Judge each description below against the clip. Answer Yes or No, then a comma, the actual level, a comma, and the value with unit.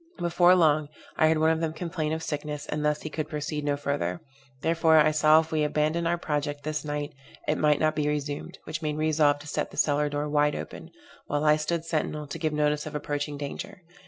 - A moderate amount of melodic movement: No, narrow, 1.2 semitones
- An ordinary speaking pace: No, fast, 225 wpm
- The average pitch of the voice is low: No, medium, 150 Hz